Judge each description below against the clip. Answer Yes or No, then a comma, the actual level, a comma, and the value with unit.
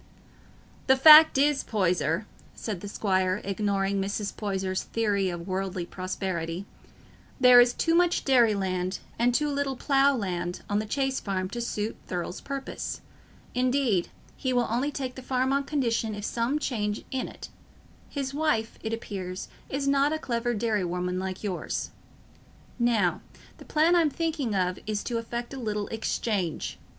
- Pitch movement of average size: No, wide, 5.7 semitones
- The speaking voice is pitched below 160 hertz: No, high, 225 Hz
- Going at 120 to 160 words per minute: Yes, average, 155 wpm